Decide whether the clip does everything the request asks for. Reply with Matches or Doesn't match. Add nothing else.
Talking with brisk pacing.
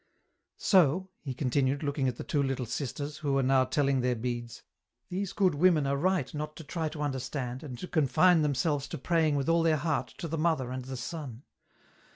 Matches